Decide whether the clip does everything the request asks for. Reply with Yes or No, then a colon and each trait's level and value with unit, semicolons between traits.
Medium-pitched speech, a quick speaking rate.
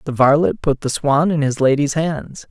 Yes: medium, 145 Hz; fast, 215 wpm